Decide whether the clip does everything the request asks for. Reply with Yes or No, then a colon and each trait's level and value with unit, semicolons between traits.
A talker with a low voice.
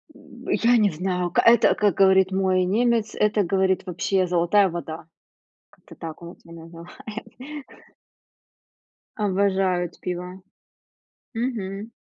No: high, 190 Hz